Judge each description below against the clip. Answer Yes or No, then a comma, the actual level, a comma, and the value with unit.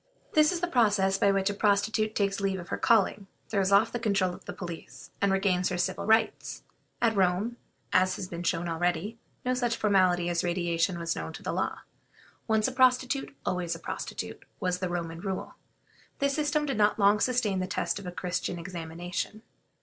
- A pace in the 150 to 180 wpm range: No, average, 195 wpm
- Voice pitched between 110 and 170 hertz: No, high, 195 Hz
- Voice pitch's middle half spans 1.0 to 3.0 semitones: No, average, 3.7 semitones